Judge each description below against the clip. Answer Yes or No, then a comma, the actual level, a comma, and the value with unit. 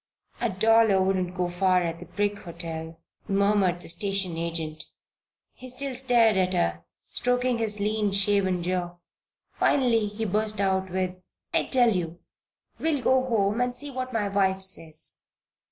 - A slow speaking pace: No, average, 155 wpm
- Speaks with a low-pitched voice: No, high, 195 Hz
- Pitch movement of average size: Yes, average, 3.9 semitones